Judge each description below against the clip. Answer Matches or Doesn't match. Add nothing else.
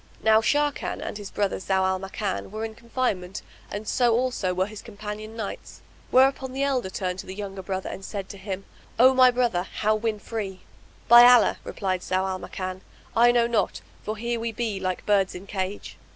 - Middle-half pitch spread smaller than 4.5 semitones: Matches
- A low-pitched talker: Doesn't match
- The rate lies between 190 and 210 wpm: Matches